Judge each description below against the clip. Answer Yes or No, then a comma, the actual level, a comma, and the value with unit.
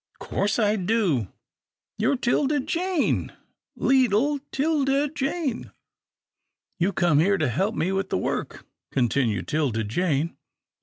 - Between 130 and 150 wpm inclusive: Yes, average, 140 wpm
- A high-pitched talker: Yes, high, 200 Hz